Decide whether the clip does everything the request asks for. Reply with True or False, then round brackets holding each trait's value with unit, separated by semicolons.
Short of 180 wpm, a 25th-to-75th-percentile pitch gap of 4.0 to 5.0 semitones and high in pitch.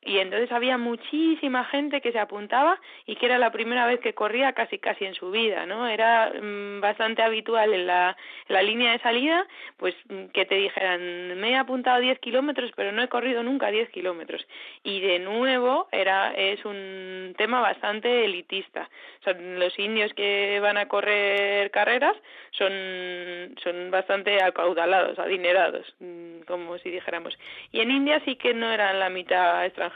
True (170 wpm; 4.4 semitones; 205 Hz)